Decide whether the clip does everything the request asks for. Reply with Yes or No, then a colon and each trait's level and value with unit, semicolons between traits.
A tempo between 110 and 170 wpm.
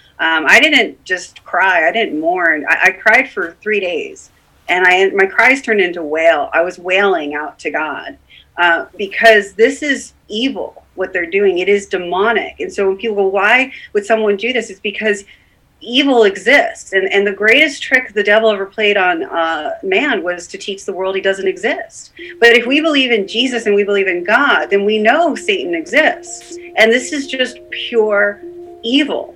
No: average, 190 wpm